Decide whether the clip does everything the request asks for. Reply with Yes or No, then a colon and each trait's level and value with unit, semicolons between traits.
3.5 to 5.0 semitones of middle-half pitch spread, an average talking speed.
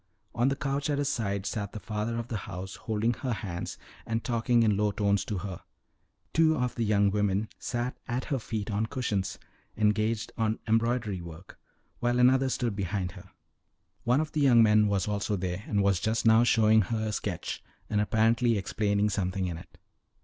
No: average, 2.9 semitones; average, 190 wpm